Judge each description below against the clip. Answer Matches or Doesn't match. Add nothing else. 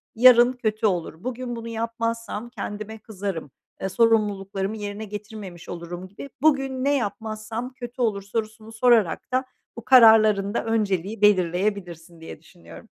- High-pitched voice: Matches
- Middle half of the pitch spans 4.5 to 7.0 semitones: Doesn't match